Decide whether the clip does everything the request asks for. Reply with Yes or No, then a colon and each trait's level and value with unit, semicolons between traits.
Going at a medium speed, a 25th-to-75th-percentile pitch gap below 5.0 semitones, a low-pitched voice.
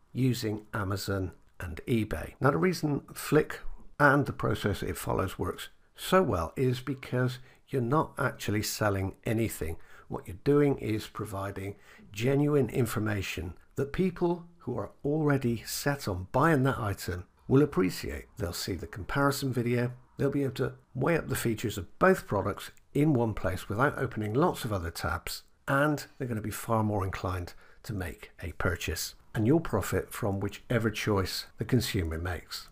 No: average, 160 wpm; wide, 5.5 semitones; low, 120 Hz